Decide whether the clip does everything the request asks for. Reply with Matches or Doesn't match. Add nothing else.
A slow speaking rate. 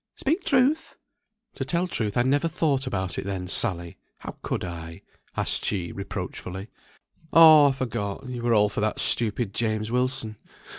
Doesn't match